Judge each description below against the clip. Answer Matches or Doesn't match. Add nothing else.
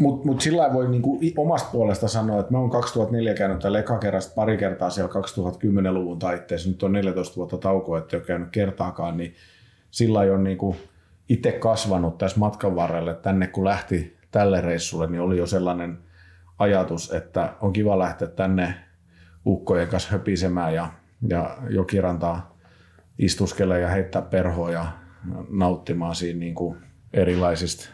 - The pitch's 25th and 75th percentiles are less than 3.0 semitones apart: Matches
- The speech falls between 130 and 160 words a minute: Matches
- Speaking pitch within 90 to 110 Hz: Matches